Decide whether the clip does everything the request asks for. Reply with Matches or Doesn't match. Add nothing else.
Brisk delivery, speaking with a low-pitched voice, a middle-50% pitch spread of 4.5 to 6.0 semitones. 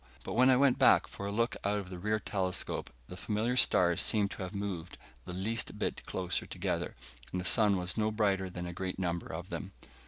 Doesn't match